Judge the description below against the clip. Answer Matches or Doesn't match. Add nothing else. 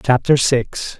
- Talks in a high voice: Doesn't match